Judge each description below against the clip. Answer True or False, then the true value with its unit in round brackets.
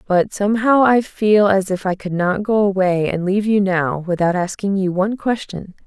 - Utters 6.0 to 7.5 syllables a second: False (5.0 syllables/s)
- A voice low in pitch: False (195 Hz)